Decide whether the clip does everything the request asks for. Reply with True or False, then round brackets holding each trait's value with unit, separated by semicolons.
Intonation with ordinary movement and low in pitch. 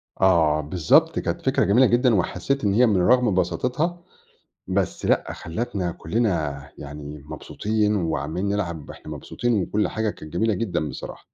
False (5.8 semitones; 95 Hz)